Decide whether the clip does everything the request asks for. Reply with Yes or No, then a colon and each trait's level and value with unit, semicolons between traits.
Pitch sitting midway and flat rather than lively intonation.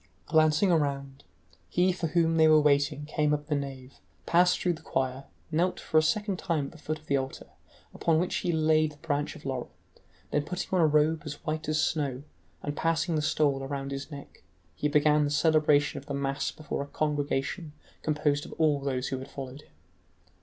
Yes: medium, 150 Hz; narrow, 2.1 semitones